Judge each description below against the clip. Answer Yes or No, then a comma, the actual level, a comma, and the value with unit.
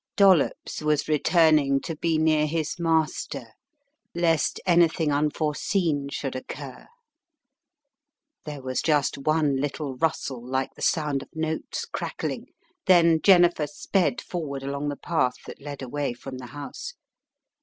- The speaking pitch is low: No, medium, 150 Hz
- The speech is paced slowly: Yes, slow, 130 wpm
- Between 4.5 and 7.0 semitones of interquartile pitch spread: No, average, 2.7 semitones